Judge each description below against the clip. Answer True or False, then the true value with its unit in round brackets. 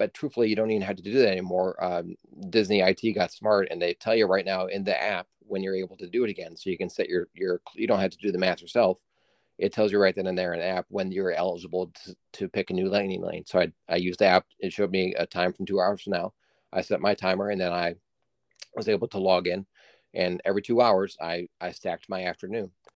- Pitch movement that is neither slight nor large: False (2.1 semitones)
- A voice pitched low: True (95 Hz)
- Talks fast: True (265 wpm)